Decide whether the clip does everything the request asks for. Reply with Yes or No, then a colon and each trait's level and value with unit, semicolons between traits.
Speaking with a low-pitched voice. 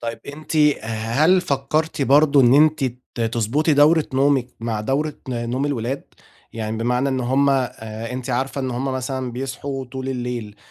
Yes: low, 130 Hz